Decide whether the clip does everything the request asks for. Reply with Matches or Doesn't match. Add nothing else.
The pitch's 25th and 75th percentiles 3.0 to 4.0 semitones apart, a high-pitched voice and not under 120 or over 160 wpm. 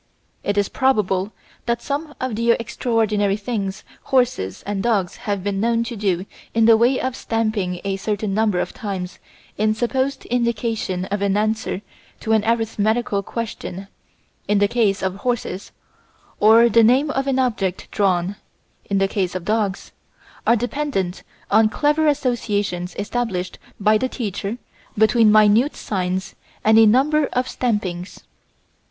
Matches